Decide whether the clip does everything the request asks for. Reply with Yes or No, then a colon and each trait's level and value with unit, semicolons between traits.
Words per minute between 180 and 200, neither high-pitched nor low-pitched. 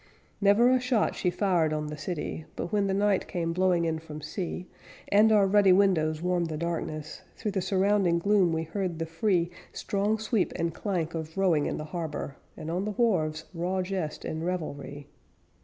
Yes: average, 190 wpm; medium, 175 Hz